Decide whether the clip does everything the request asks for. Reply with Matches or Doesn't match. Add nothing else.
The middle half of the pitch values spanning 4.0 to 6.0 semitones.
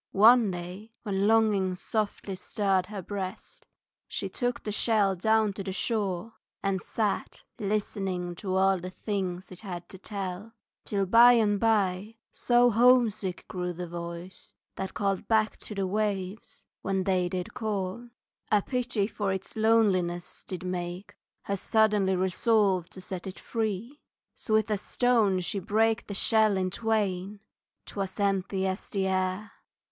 Doesn't match